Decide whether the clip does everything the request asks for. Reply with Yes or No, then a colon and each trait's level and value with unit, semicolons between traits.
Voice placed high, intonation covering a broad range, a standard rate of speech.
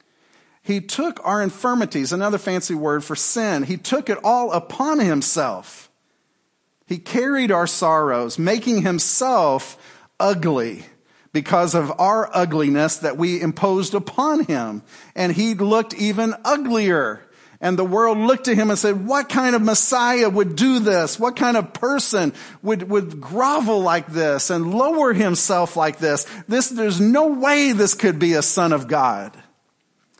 Yes: high, 205 Hz; wide, 5.7 semitones; average, 150 wpm